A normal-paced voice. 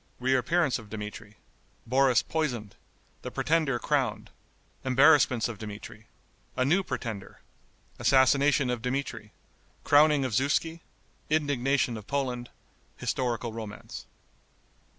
No: slow, 100 wpm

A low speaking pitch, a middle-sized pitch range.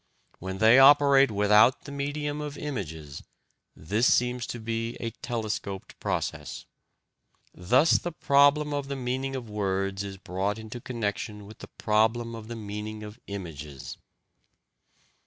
Yes: low, 110 Hz; average, 4.9 semitones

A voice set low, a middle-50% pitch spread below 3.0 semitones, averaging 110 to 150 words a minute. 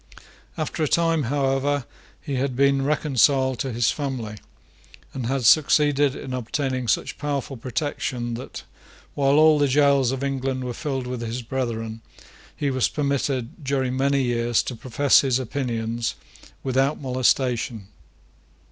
Yes: low, 130 Hz; narrow, 2.4 semitones; average, 140 wpm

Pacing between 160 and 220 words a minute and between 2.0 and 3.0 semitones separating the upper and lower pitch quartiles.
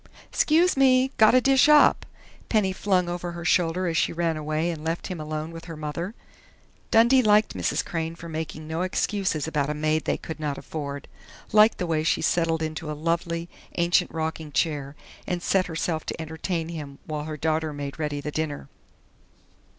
Yes: average, 180 wpm; average, 2.7 semitones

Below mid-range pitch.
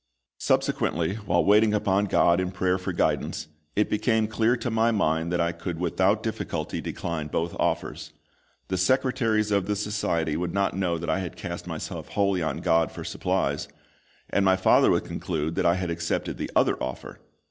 Yes: very low, 95 Hz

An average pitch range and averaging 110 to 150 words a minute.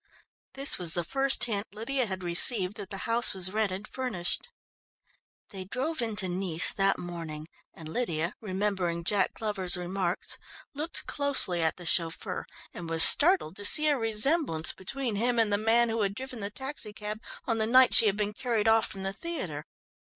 No: average, 4.7 semitones; average, 175 wpm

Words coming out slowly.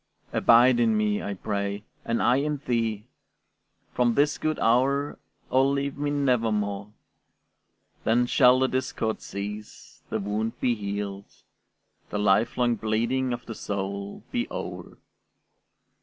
Yes: slow, 125 wpm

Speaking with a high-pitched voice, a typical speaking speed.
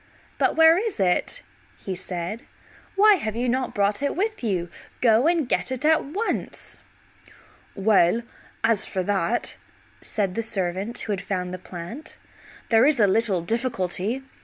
Yes: high, 225 Hz; average, 155 wpm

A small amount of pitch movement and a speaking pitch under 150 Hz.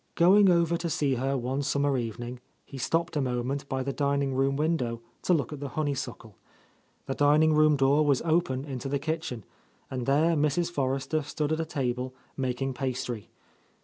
No: average, 3.0 semitones; medium, 140 Hz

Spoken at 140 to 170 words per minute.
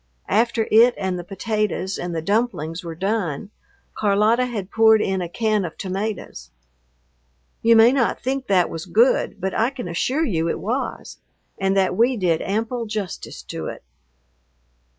Yes: average, 160 wpm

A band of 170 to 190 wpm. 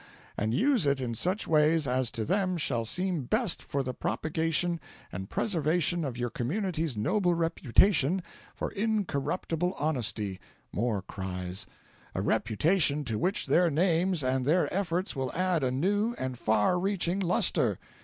No: average, 145 wpm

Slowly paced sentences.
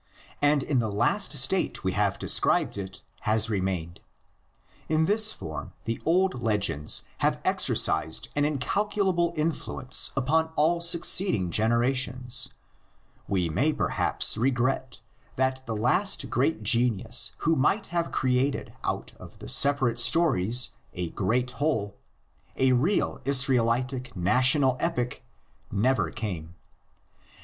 Yes: slow, 120 wpm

